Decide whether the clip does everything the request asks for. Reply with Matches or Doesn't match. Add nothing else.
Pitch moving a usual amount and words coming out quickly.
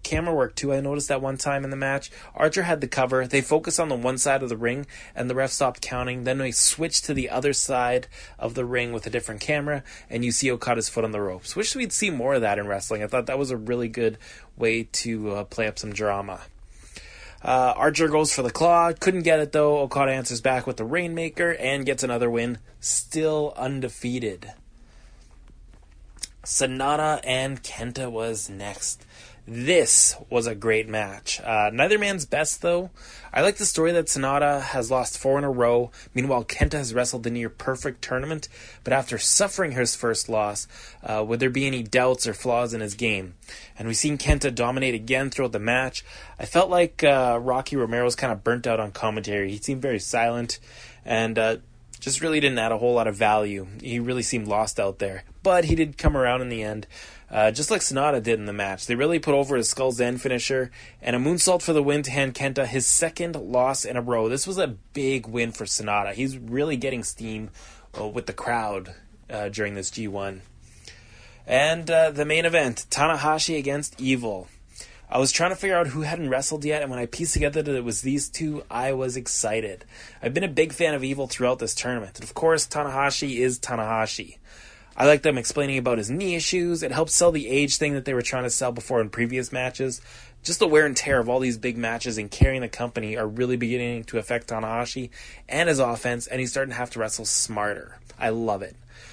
Matches